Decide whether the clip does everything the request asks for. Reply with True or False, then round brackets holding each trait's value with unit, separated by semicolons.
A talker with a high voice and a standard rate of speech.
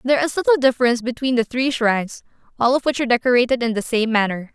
False (245 Hz; 225 wpm)